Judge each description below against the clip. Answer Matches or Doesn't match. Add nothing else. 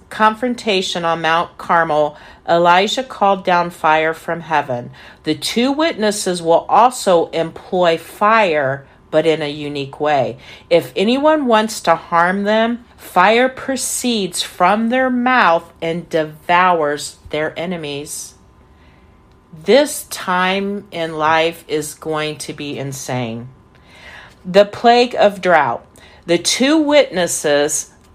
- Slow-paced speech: Matches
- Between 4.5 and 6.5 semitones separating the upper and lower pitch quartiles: Matches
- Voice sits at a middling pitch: Matches